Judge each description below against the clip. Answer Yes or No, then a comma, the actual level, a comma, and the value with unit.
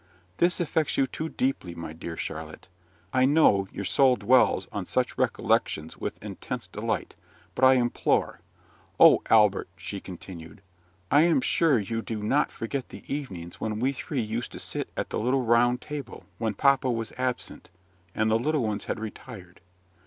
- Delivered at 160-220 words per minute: Yes, average, 170 wpm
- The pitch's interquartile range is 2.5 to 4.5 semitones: No, average, 5.0 semitones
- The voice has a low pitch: Yes, low, 115 Hz